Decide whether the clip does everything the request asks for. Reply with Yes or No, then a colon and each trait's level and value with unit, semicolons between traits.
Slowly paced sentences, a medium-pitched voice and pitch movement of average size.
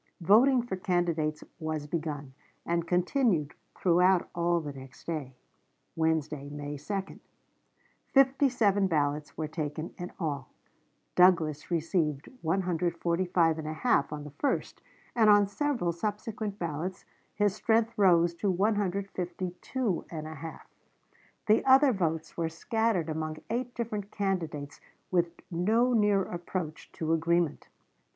Yes: slow, 115 wpm; medium, 175 Hz; average, 4.4 semitones